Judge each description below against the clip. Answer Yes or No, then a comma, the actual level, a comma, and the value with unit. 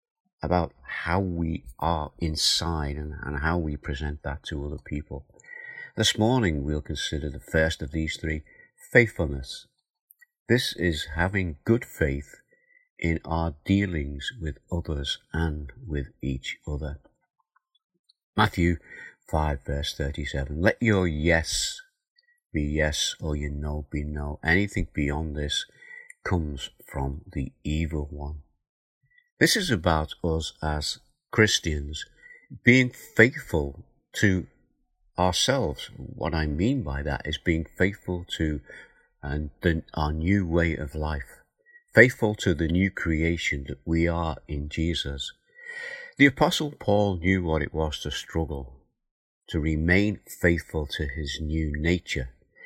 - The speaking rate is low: Yes, slow, 125 wpm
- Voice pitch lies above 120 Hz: No, very low, 80 Hz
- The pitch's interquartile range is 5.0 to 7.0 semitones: Yes, wide, 5.6 semitones